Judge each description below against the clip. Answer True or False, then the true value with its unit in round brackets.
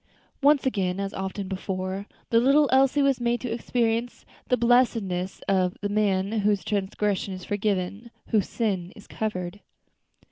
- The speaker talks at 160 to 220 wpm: False (145 wpm)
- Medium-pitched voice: False (205 Hz)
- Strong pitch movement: False (3.9 semitones)